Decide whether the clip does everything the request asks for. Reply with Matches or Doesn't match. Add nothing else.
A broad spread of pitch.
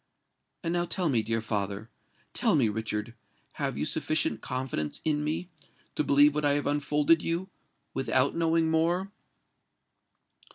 Matches